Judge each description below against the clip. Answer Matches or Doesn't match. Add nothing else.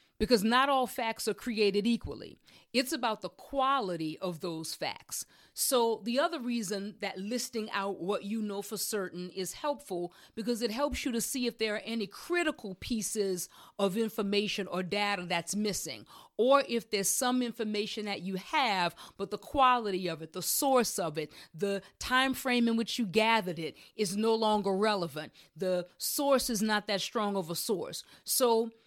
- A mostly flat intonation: Doesn't match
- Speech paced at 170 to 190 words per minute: Matches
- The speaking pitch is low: Doesn't match